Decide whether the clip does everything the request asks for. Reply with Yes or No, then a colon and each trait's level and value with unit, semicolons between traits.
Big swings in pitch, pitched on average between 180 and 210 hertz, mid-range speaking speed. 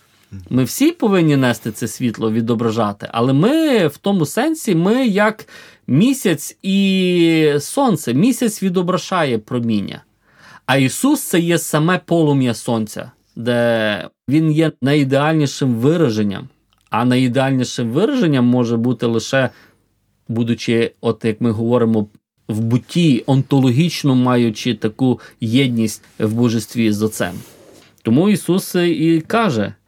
No: wide, 6.6 semitones; low, 130 Hz; average, 115 wpm